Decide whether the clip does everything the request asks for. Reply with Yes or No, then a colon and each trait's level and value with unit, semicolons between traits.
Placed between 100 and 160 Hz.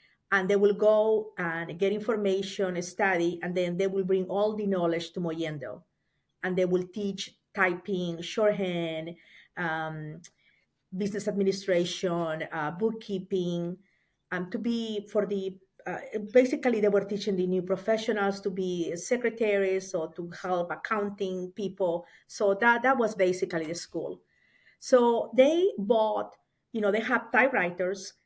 No: high, 195 Hz